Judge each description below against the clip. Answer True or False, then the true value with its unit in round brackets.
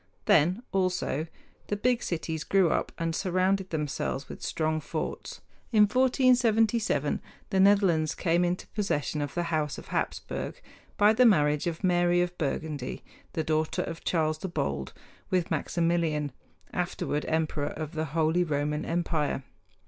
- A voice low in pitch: False (165 Hz)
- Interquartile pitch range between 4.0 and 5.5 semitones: False (3.6 semitones)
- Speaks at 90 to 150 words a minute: True (140 wpm)